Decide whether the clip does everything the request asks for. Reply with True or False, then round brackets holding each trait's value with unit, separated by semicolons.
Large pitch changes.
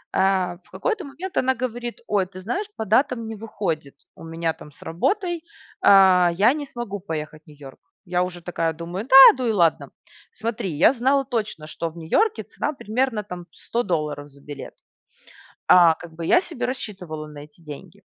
True (6.9 semitones)